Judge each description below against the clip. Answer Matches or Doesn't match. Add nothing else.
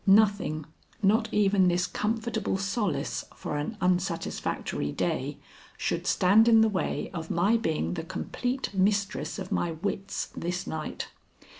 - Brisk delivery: Doesn't match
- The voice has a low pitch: Doesn't match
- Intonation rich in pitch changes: Doesn't match